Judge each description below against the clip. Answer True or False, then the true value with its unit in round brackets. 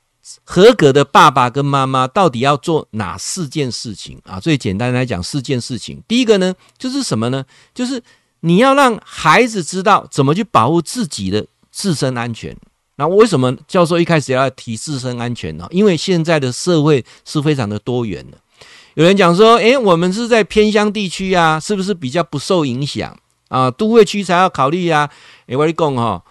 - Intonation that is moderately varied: False (7.1 semitones)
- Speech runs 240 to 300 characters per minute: True (285 characters per minute)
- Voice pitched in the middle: True (150 Hz)